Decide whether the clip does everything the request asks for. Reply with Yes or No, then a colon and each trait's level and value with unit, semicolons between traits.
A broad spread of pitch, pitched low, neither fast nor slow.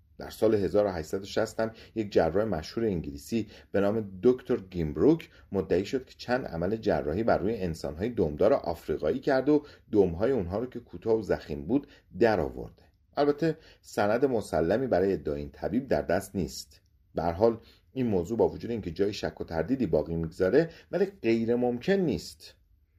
No: wide, 5.8 semitones; low, 100 Hz; fast, 160 wpm